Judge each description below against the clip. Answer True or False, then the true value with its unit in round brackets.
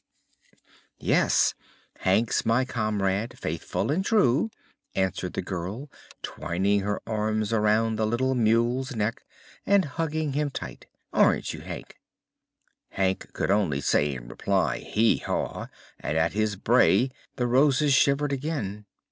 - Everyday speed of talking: False (130 wpm)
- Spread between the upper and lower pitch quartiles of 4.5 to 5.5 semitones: True (4.9 semitones)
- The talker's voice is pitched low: True (115 Hz)